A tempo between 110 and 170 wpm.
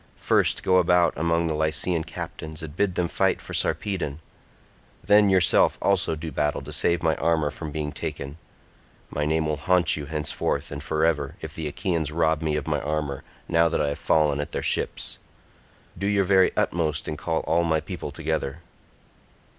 No: average, 185 wpm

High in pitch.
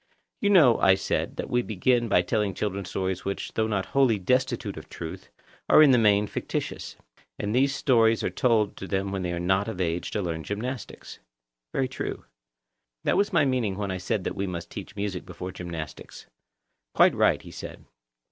No: low, 100 Hz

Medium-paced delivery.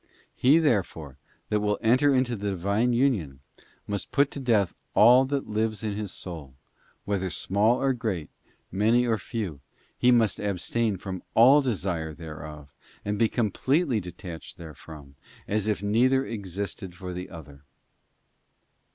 Yes: average, 150 wpm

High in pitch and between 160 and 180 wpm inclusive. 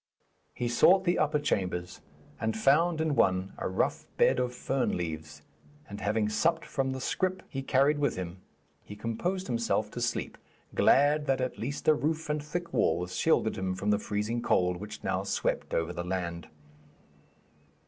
No: low, 115 Hz; average, 170 wpm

